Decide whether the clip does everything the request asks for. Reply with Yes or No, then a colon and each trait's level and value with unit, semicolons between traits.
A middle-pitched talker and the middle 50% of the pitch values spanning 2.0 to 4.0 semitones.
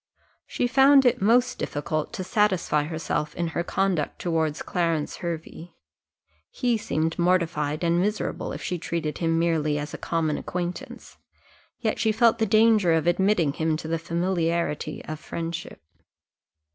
Yes: medium, 170 Hz; average, 3.5 semitones